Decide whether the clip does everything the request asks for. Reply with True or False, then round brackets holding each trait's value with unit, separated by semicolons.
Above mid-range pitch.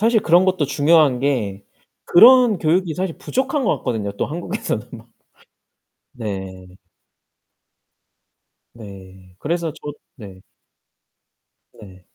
False (145 Hz)